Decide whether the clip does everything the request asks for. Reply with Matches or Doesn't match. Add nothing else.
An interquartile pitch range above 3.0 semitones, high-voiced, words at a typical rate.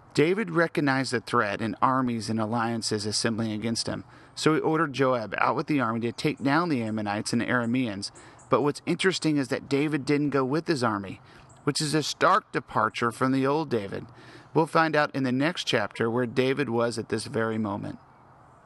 Doesn't match